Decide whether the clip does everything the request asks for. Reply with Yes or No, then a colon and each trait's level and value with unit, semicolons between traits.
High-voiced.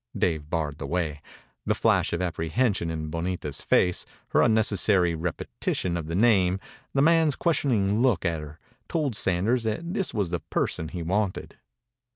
No: very low, 90 Hz